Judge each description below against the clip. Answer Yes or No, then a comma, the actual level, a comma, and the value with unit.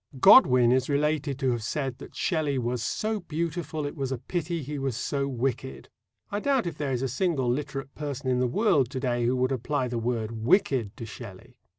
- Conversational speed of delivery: No, fast, 210 wpm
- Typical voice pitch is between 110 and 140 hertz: Yes, low, 135 Hz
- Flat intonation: No, average, 3.3 semitones